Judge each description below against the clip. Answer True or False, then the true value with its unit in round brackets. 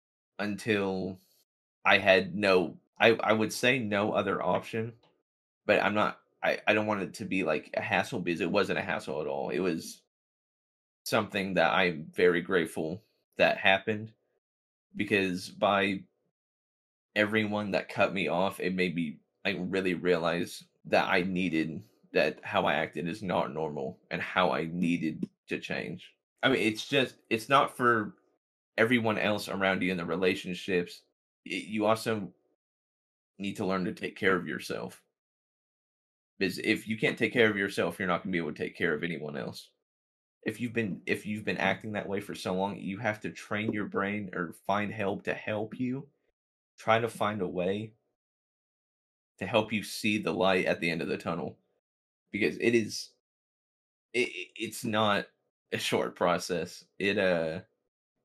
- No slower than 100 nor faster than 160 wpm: False (170 wpm)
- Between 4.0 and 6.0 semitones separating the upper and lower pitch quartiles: False (3.4 semitones)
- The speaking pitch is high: False (100 Hz)